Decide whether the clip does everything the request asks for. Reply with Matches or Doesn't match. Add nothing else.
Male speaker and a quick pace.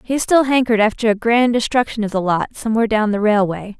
Doesn't match